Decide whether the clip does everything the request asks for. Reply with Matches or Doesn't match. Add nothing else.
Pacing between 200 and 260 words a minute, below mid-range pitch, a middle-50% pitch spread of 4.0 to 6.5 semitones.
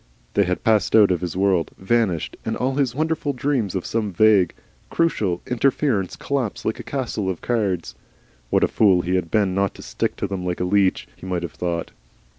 Matches